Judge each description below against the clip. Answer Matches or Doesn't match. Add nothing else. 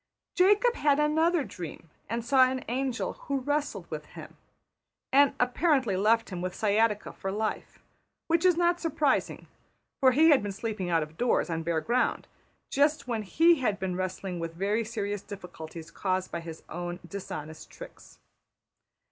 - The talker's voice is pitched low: Doesn't match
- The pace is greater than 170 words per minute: Doesn't match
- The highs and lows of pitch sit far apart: Matches